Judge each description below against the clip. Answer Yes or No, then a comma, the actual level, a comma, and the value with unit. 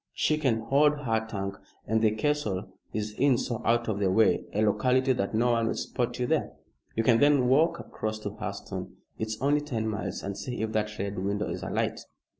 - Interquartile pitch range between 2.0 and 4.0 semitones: Yes, average, 3.5 semitones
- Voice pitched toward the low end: Yes, low, 110 Hz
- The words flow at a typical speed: No, fast, 210 wpm